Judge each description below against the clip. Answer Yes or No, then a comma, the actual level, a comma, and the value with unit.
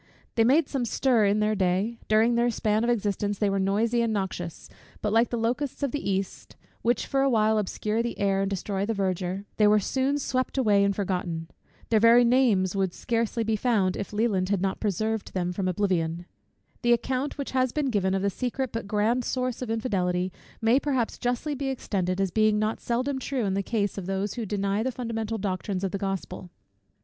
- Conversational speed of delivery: No, fast, 210 wpm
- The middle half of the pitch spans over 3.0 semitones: Yes, average, 3.6 semitones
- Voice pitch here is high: Yes, high, 215 Hz